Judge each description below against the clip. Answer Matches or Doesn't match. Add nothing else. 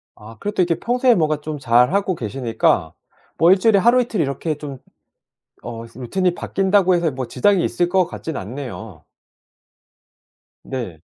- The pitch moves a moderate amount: Doesn't match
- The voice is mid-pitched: Matches